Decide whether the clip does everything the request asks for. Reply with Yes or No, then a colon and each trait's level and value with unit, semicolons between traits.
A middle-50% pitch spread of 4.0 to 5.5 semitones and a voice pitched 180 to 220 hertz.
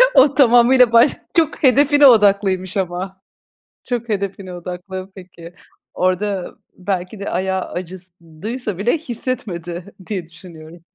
Yes: average, 4.7 semitones; high, 190 Hz